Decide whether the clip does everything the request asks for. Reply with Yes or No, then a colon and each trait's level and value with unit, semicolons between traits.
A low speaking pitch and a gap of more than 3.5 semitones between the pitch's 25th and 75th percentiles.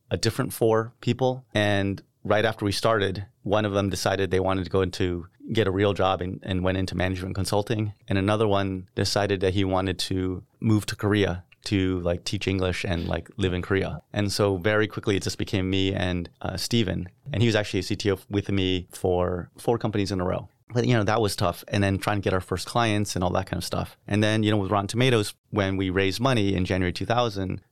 No: low, 100 Hz; narrow, 2.4 semitones